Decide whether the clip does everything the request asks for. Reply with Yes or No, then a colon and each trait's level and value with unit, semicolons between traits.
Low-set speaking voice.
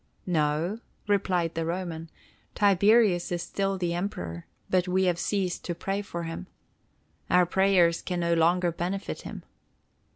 No: medium, 180 Hz